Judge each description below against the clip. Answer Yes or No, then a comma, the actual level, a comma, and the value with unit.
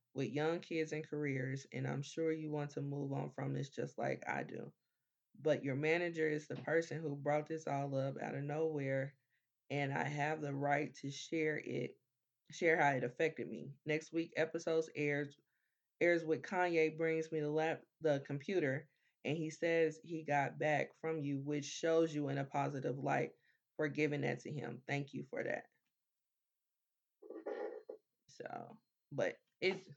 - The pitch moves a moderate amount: No, narrow, 2.3 semitones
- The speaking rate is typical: Yes, average, 170 wpm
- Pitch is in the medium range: Yes, medium, 150 Hz